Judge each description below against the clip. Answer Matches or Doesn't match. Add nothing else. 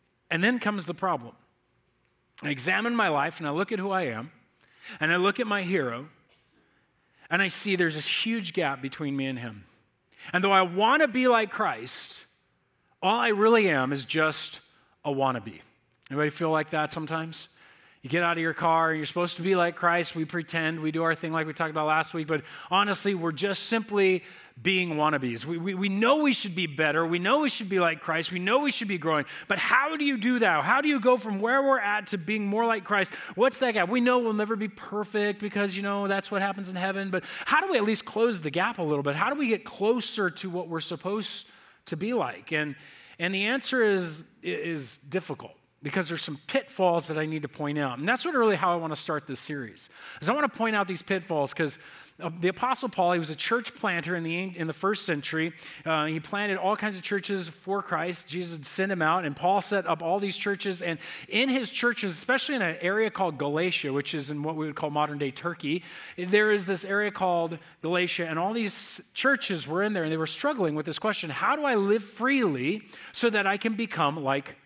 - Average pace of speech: Doesn't match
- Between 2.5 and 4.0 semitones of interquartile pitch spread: Doesn't match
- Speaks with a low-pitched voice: Doesn't match